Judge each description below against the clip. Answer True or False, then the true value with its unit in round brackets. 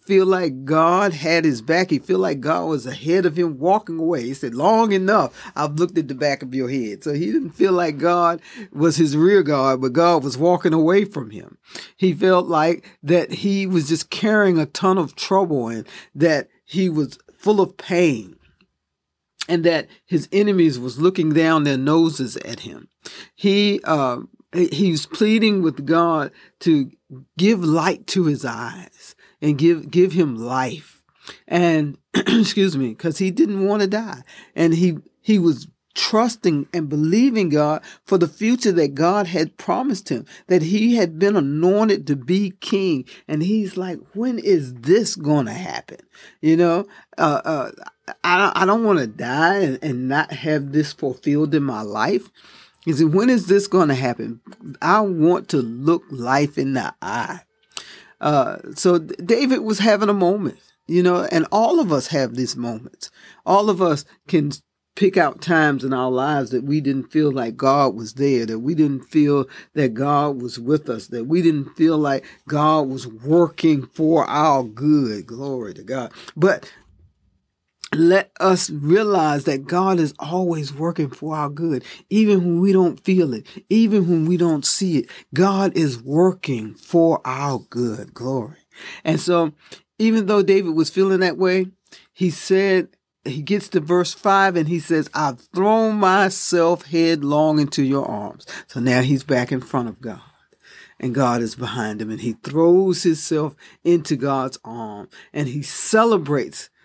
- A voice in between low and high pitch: True (165 Hz)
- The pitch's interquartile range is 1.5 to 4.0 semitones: False (5.0 semitones)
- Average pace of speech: True (170 wpm)